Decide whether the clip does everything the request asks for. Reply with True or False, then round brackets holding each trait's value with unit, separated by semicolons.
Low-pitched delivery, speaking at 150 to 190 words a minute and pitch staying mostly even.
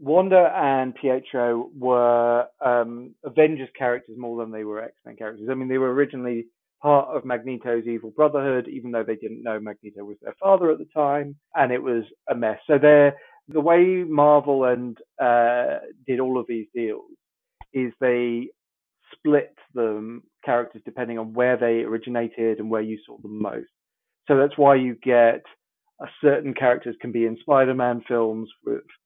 False (125 Hz; 170 wpm; 3.4 semitones)